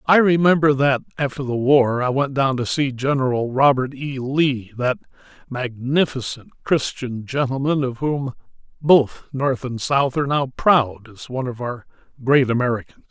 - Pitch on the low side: Yes, low, 130 Hz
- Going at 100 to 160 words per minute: Yes, average, 155 wpm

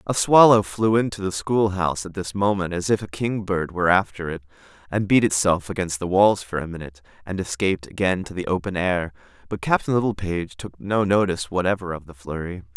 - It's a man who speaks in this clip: Yes, male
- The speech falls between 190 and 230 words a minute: Yes, average, 195 wpm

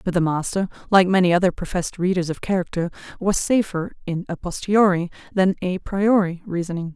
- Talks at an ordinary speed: Yes, average, 165 wpm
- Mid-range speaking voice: Yes, medium, 180 Hz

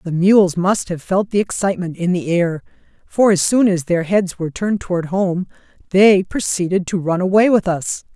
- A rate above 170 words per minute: Yes, average, 200 wpm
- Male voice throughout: No, female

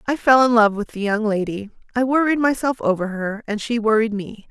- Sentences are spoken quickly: Yes, fast, 225 wpm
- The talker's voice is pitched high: Yes, high, 225 Hz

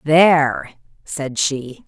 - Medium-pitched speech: Yes, medium, 145 Hz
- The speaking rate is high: No, slow, 95 wpm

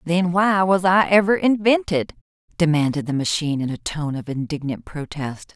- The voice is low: No, medium, 165 Hz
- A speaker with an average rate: Yes, average, 160 wpm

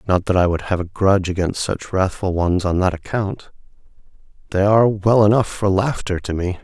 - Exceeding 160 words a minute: Yes, average, 200 wpm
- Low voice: Yes, very low, 95 Hz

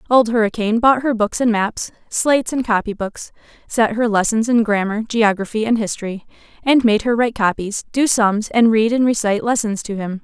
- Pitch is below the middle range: No, high, 220 Hz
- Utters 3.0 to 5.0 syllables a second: No, 5.4 syllables/s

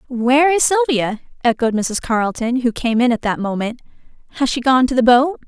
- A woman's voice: Yes, female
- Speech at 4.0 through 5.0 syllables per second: No, 5.5 syllables/s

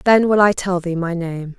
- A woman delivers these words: Yes, female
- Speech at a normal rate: No, fast, 265 wpm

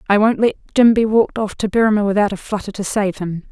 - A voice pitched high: Yes, high, 205 Hz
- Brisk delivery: Yes, fast, 255 wpm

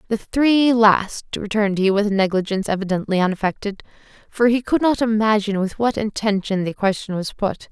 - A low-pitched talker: No, high, 210 Hz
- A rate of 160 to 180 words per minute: Yes, average, 170 wpm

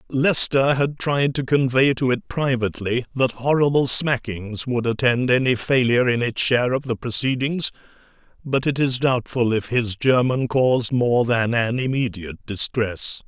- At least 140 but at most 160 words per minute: Yes, average, 155 wpm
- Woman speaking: No, male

